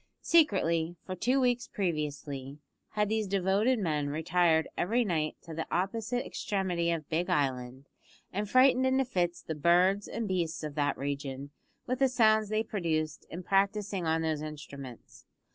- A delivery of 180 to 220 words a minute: No, average, 155 wpm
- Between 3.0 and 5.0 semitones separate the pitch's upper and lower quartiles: No, wide, 5.5 semitones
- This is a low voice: No, medium, 175 Hz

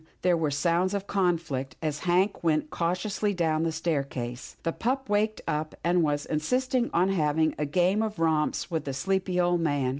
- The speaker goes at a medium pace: Yes, average, 190 wpm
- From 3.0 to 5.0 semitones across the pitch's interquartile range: Yes, average, 3.9 semitones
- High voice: No, medium, 170 Hz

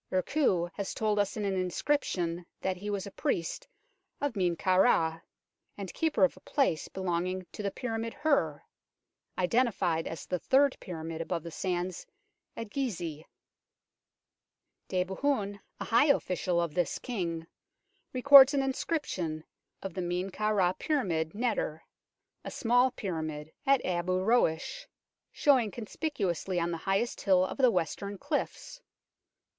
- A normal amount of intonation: No, wide, 6.1 semitones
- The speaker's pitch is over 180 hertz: Yes, high, 190 Hz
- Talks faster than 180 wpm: No, average, 140 wpm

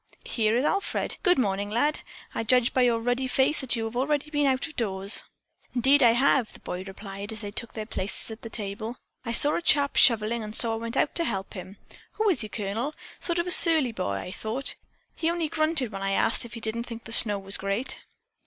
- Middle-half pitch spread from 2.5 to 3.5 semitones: No, average, 4.6 semitones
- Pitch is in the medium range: No, high, 235 Hz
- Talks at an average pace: No, fast, 235 wpm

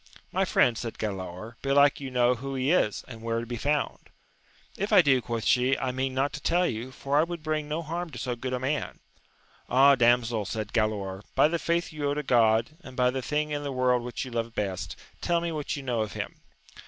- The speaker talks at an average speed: No, fast, 235 wpm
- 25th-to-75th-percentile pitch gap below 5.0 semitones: Yes, average, 4.0 semitones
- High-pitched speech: No, low, 130 Hz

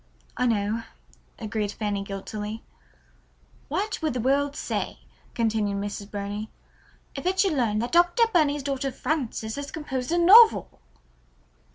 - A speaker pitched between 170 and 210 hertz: No, high, 245 Hz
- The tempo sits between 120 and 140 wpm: Yes, slow, 135 wpm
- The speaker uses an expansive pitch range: Yes, wide, 6.2 semitones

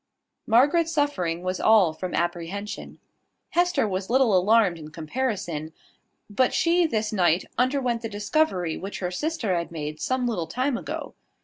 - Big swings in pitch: Yes, wide, 6.7 semitones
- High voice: Yes, high, 205 Hz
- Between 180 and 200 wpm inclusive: No, average, 145 wpm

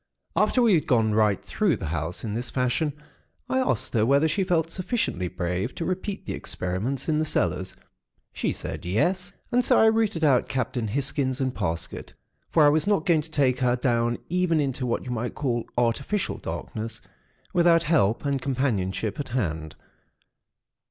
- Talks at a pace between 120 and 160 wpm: No, average, 175 wpm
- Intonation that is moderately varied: No, wide, 6.8 semitones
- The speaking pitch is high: No, low, 130 Hz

